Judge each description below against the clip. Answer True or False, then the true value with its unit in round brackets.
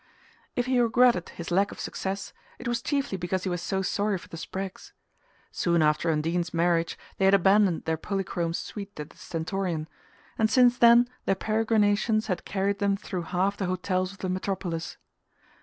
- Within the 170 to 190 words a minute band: True (175 wpm)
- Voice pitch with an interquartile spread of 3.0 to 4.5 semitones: True (3.3 semitones)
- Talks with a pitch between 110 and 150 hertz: False (190 Hz)